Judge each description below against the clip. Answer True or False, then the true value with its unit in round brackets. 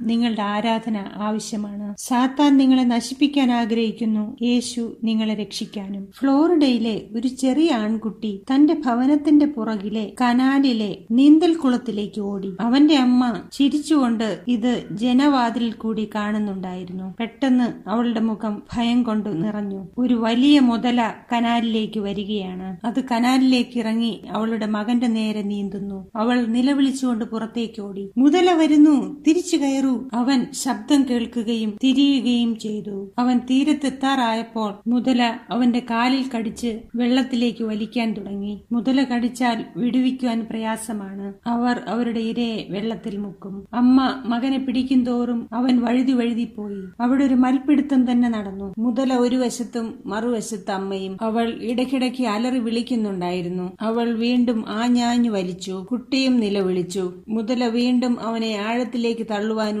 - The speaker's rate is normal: True (110 wpm)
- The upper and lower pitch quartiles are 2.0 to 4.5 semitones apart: True (2.7 semitones)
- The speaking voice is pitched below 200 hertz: False (235 Hz)